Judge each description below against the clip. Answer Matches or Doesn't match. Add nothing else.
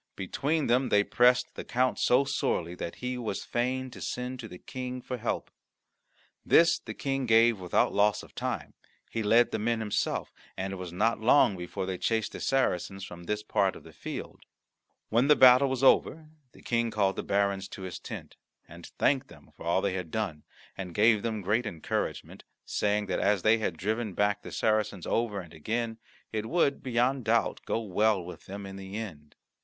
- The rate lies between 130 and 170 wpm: Doesn't match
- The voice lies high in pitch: Doesn't match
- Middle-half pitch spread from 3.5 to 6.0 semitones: Matches